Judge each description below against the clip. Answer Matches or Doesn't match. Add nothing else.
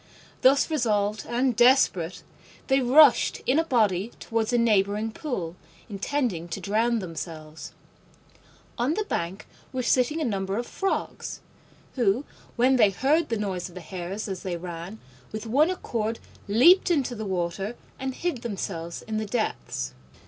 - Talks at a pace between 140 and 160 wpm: Matches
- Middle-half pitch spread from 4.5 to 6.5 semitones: Matches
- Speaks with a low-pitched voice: Doesn't match